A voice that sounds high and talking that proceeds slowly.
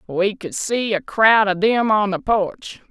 No: high, 205 Hz; fast, 205 wpm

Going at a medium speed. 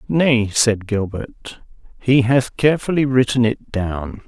No: slow, 125 wpm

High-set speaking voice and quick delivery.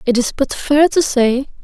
Yes: very high, 270 Hz; fast, 220 wpm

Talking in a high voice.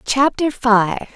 Yes: high, 245 Hz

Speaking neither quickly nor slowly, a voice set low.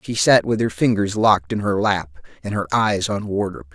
No: fast, 225 wpm; low, 100 Hz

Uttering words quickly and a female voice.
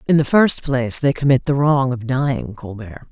Yes: fast, 210 wpm; female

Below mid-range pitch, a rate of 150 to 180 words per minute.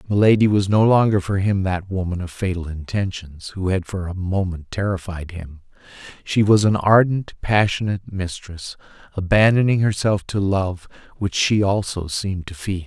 Yes: very low, 95 Hz; average, 160 wpm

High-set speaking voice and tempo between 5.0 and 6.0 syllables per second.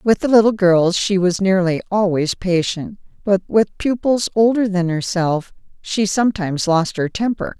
No: high, 195 Hz; 4.5 syllables/s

